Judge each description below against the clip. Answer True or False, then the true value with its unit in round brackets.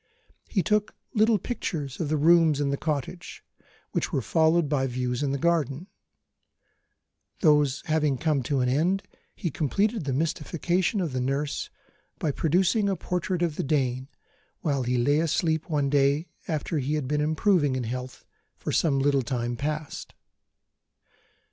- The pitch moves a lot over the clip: False (3.7 semitones)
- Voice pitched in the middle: True (150 Hz)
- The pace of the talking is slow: False (155 wpm)